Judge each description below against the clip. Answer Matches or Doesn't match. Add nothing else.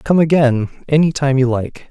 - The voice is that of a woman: Doesn't match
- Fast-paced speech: Doesn't match